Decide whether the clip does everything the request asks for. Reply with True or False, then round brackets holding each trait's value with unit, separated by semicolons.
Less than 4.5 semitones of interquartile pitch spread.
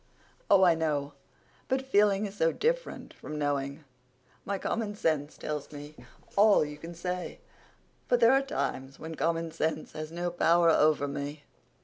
False (5.1 semitones)